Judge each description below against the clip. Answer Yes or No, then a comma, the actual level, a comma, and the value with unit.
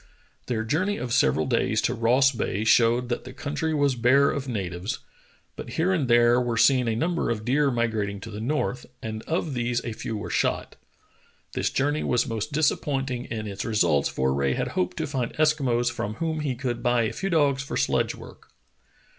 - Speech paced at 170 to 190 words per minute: No, average, 200 wpm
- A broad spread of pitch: No, average, 3.9 semitones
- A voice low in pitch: Yes, low, 120 Hz